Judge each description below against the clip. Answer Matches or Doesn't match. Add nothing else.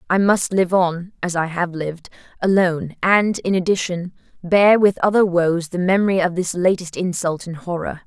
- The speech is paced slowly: Doesn't match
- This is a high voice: Doesn't match